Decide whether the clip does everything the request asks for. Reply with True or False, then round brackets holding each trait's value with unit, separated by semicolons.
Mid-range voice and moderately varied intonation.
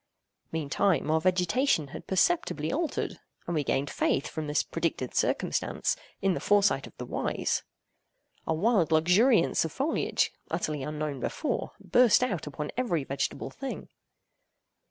False (165 Hz; 6.3 semitones)